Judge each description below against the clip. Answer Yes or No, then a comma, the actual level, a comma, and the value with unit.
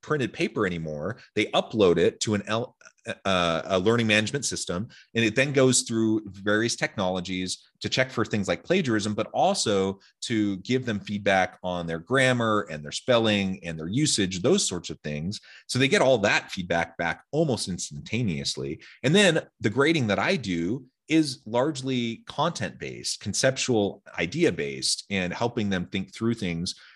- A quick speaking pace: No, average, 165 wpm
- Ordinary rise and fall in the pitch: Yes, average, 4.6 semitones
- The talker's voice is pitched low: Yes, low, 105 Hz